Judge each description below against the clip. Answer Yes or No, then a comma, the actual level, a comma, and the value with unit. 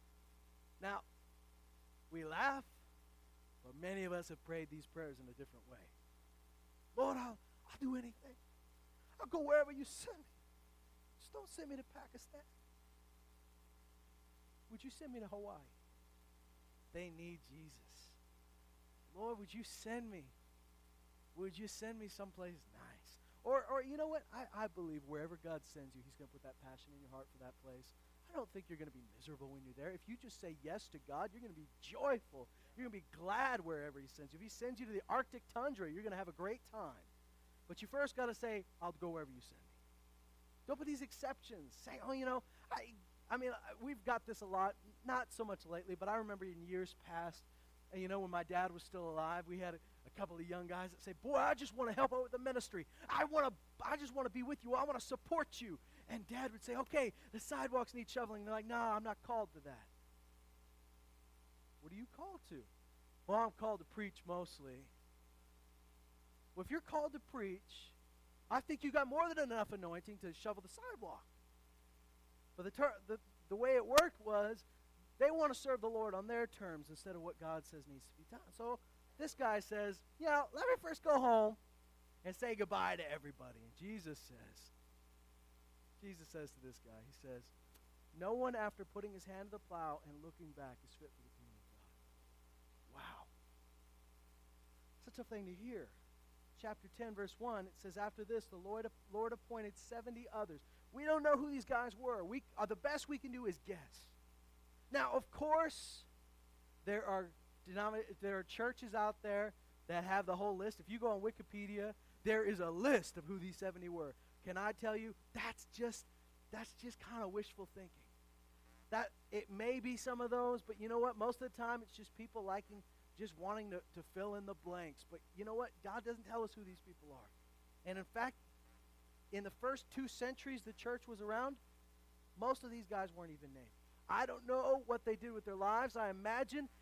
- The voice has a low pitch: No, high, 190 Hz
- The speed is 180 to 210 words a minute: Yes, fast, 205 wpm